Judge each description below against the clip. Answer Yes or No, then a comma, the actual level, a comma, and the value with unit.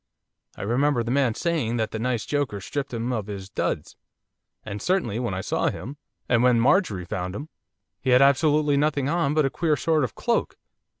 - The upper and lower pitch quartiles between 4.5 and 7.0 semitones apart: Yes, average, 4.8 semitones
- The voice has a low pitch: Yes, low, 125 Hz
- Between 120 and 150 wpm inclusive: No, average, 195 wpm